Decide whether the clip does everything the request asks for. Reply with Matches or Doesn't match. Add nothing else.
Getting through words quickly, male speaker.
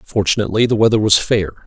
Doesn't match